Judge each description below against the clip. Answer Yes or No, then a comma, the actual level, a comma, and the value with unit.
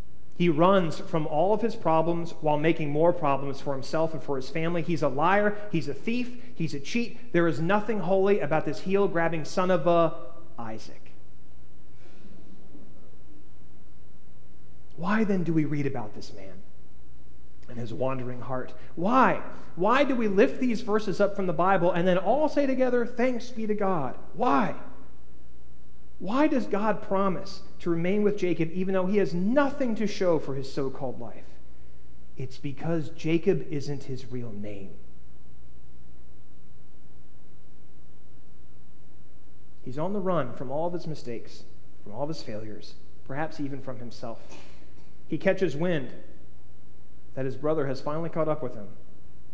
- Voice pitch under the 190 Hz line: Yes, medium, 140 Hz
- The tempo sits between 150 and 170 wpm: Yes, average, 155 wpm